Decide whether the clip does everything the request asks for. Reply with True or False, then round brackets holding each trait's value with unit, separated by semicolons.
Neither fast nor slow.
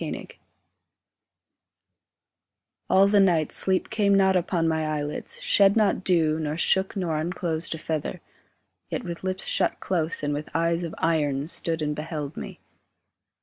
True (150 wpm)